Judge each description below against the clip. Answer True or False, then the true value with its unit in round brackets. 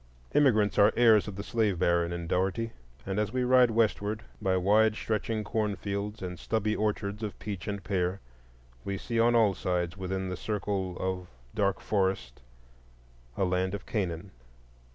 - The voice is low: True (100 Hz)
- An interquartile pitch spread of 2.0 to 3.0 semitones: True (2.6 semitones)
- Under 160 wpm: False (170 wpm)